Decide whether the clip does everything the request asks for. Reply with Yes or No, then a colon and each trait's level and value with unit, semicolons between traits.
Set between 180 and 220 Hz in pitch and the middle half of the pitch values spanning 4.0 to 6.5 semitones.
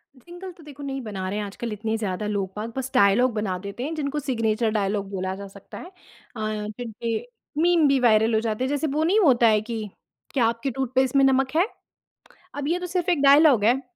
No: high, 240 Hz; average, 4.9 semitones